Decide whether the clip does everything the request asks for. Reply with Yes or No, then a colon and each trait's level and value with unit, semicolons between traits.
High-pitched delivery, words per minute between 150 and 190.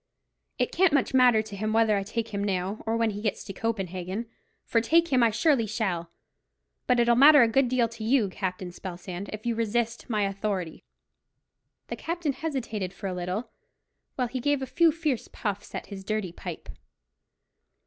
Yes: high, 220 Hz; average, 185 wpm